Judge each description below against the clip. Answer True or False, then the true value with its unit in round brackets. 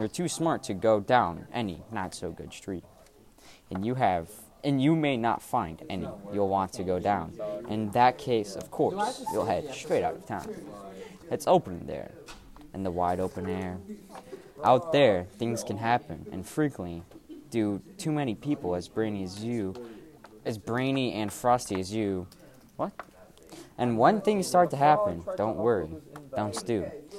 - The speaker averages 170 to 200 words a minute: True (180 wpm)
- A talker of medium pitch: False (110 Hz)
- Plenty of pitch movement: True (6.0 semitones)